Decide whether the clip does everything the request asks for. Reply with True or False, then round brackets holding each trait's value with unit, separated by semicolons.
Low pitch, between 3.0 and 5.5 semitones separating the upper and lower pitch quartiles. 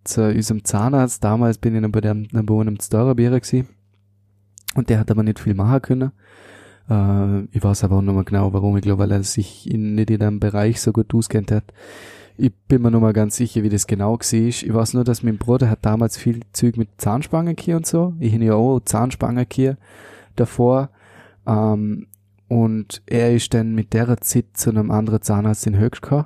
False (110 Hz; 2.6 semitones)